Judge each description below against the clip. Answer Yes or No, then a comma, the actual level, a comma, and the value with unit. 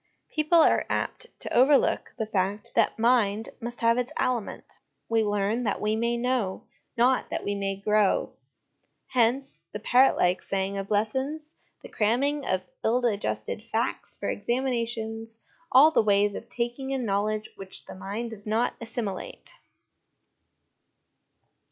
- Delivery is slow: No, average, 145 wpm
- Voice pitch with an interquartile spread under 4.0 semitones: Yes, average, 3.4 semitones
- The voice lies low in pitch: No, high, 225 Hz